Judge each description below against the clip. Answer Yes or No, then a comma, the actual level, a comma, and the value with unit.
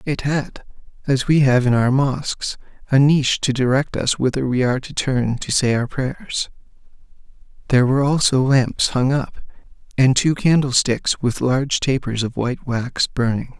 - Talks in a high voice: No, low, 130 Hz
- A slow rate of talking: No, average, 170 wpm